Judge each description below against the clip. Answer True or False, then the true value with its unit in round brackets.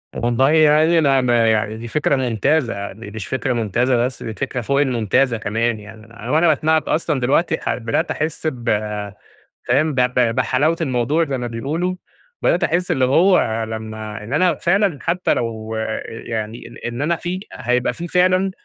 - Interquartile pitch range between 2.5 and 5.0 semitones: False (5.4 semitones)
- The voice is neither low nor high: False (125 Hz)